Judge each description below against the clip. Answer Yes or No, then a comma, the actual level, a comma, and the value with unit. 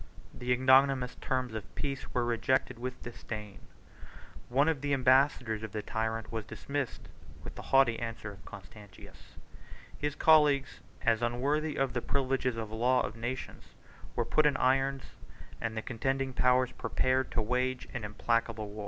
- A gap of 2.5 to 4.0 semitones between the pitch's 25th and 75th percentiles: Yes, average, 2.9 semitones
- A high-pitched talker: No, low, 125 Hz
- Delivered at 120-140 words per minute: No, average, 160 wpm